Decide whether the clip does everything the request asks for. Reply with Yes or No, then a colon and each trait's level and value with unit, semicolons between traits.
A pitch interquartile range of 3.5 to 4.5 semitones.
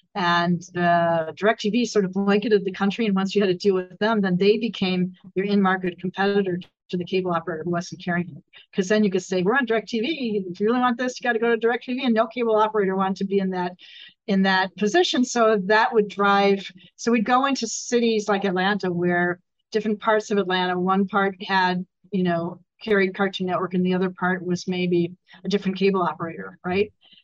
No: average, 2.9 semitones